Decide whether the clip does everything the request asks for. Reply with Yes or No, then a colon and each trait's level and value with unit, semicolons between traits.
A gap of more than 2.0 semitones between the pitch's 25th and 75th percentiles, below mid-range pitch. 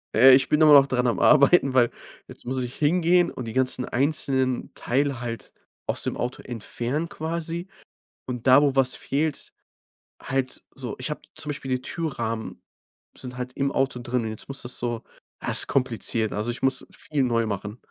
Yes: average, 2.9 semitones; low, 130 Hz